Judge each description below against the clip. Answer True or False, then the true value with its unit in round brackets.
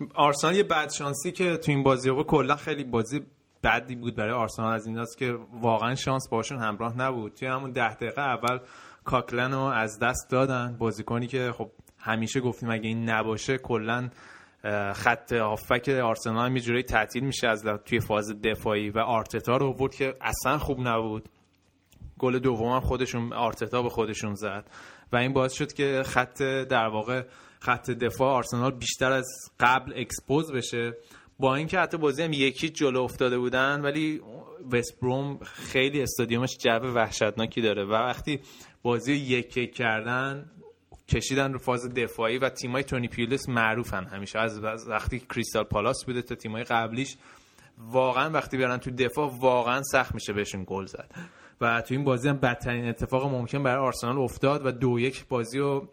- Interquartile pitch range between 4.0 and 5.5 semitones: False (2.8 semitones)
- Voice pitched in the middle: False (125 Hz)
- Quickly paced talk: True (165 wpm)